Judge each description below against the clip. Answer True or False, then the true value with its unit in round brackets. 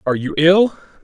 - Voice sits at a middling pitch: True (165 Hz)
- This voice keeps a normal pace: True (175 wpm)